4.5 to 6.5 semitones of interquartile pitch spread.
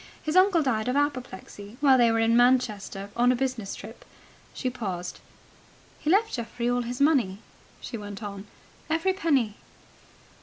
Yes: average, 4.9 semitones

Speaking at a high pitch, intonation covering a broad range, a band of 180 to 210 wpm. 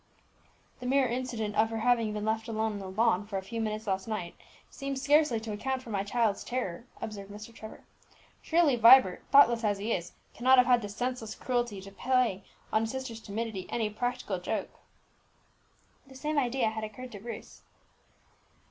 No: high, 225 Hz; average, 3.2 semitones; average, 185 wpm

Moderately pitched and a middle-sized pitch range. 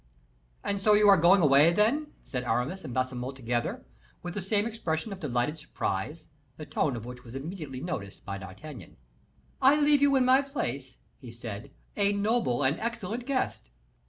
No: medium, 155 Hz; wide, 9.0 semitones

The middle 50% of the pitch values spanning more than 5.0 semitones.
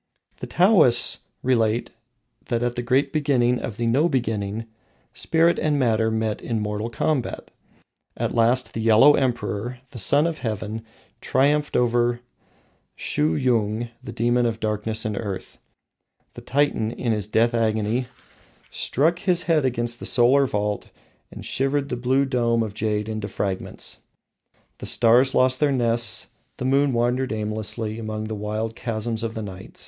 No: average, 3.0 semitones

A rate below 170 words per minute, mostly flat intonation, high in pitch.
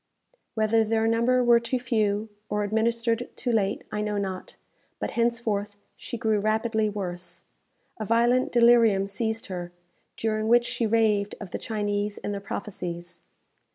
Yes: average, 150 wpm; narrow, 2.2 semitones; high, 220 Hz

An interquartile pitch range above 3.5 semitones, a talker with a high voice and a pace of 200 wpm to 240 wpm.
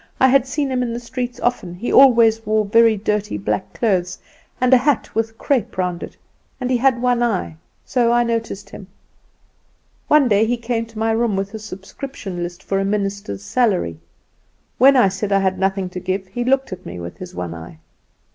Yes: average, 4.4 semitones; high, 220 Hz; fast, 205 wpm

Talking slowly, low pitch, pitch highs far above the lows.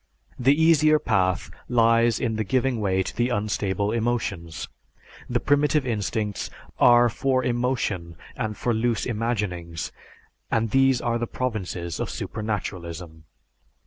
No: slow, 125 wpm; low, 115 Hz; average, 4.3 semitones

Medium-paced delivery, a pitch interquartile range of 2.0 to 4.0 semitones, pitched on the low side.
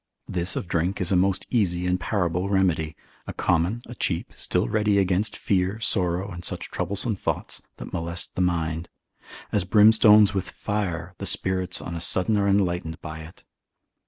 Yes: average, 170 wpm; narrow, 2.6 semitones; very low, 90 Hz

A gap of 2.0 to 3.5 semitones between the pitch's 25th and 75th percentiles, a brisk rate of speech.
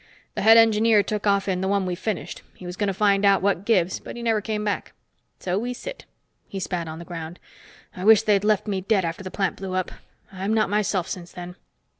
Yes: narrow, 2.6 semitones; fast, 235 wpm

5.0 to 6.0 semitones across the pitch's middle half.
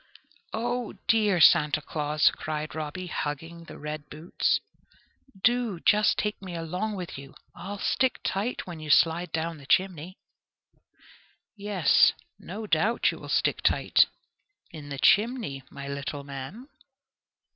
Yes: wide, 5.4 semitones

